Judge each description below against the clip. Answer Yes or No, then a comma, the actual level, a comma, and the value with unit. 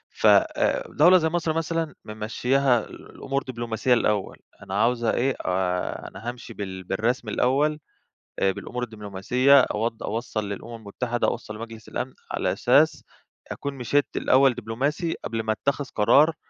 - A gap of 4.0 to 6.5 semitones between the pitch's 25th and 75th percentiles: Yes, average, 4.3 semitones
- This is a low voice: Yes, low, 120 Hz